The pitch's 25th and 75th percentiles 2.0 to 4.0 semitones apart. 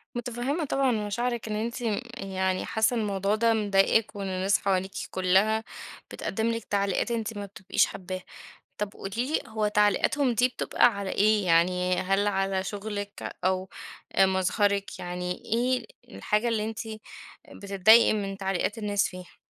Yes: narrow, 2.5 semitones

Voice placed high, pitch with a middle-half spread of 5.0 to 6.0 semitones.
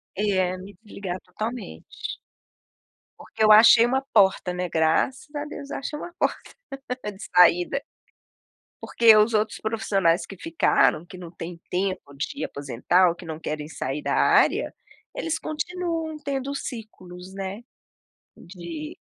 Yes: high, 195 Hz; average, 5.3 semitones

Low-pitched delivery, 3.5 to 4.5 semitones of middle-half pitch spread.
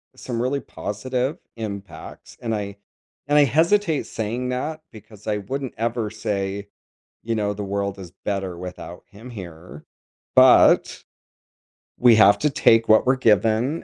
Yes: low, 110 Hz; average, 4.0 semitones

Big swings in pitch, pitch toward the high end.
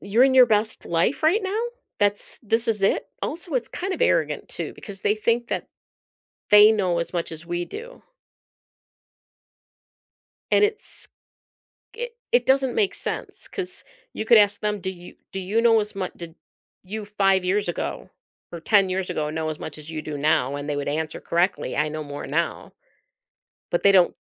Yes: wide, 5.7 semitones; high, 200 Hz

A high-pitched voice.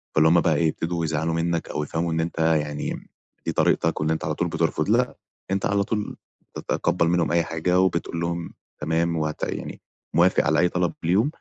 No: very low, 85 Hz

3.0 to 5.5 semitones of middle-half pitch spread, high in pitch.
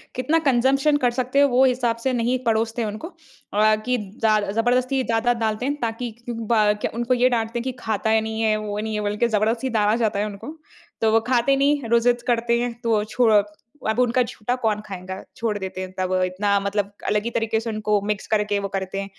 No: narrow, 2.6 semitones; high, 225 Hz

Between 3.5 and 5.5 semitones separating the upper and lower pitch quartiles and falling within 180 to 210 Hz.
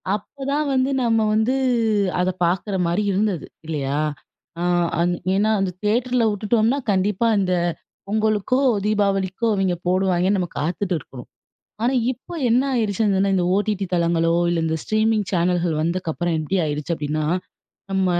Yes: average, 3.8 semitones; high, 195 Hz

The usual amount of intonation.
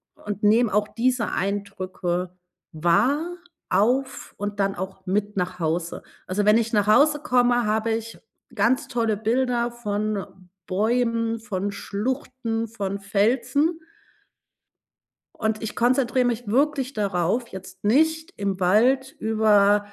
Yes: average, 3.6 semitones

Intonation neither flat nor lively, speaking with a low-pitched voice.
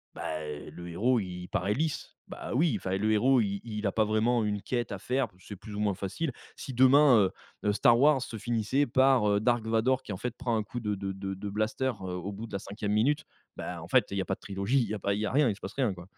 Yes: average, 4.0 semitones; low, 110 Hz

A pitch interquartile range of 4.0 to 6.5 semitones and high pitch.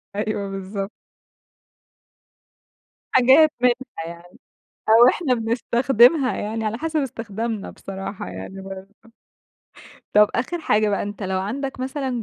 Yes: average, 4.6 semitones; high, 225 Hz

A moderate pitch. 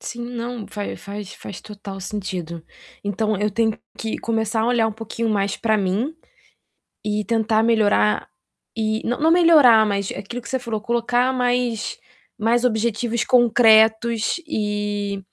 No: high, 220 Hz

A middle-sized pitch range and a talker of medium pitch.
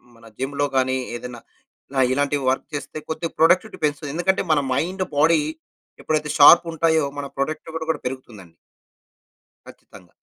Yes: average, 3.4 semitones; medium, 145 Hz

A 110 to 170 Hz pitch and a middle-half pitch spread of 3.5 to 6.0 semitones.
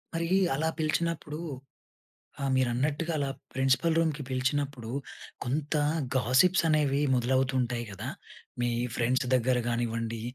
Yes: low, 135 Hz; average, 3.8 semitones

